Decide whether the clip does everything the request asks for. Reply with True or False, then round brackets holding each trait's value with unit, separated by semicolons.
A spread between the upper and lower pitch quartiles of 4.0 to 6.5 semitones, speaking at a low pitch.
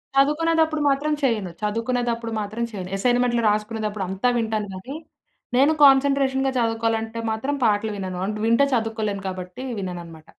False (4.3 semitones; 225 Hz)